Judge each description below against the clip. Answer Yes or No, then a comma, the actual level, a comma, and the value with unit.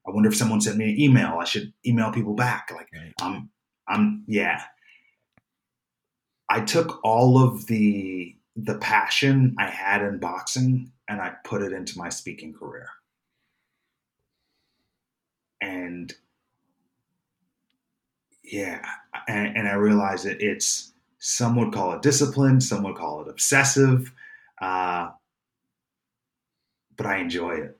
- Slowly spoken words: Yes, slow, 125 wpm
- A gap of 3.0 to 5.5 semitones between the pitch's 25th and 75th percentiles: Yes, average, 4.5 semitones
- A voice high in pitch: No, low, 115 Hz